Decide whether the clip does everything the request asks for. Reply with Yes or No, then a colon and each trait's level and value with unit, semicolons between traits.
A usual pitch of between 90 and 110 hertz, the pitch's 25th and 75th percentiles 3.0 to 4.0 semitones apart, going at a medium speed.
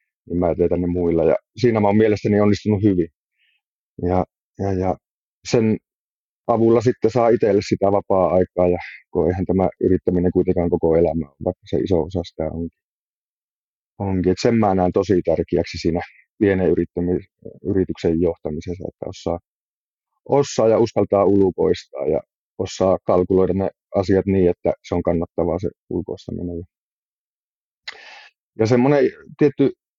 Yes: very low, 95 Hz; average, 3.7 semitones; average, 140 wpm